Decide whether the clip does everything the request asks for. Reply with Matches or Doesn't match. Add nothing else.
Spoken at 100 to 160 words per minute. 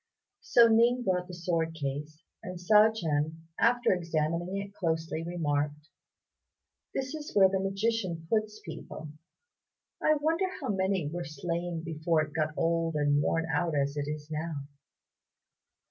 Matches